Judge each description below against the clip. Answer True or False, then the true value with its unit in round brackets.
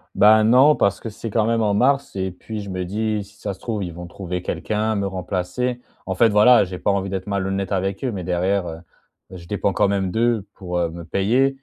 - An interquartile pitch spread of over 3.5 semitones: False (3.0 semitones)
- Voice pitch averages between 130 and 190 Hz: False (100 Hz)